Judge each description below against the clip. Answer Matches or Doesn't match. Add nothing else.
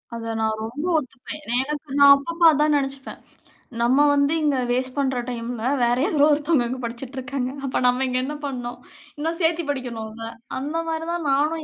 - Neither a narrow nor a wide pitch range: Matches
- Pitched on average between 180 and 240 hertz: Doesn't match